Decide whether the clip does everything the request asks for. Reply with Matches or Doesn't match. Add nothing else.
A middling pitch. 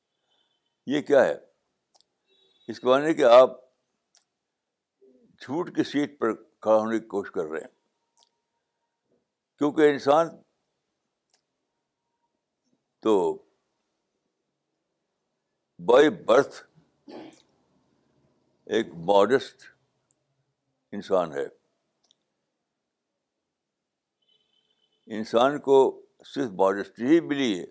Matches